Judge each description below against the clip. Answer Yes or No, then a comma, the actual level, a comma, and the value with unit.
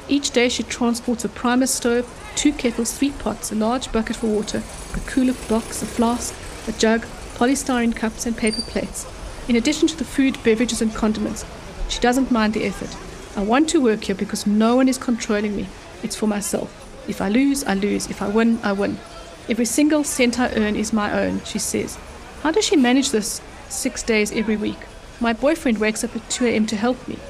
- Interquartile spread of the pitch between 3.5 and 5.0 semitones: No, average, 2.8 semitones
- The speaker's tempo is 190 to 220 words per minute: Yes, fast, 205 wpm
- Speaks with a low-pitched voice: No, high, 235 Hz